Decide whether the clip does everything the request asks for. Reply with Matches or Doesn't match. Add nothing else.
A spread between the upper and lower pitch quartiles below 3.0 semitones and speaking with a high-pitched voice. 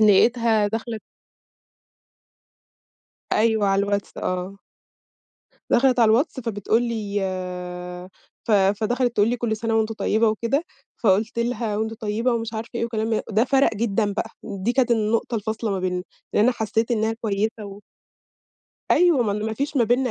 Matches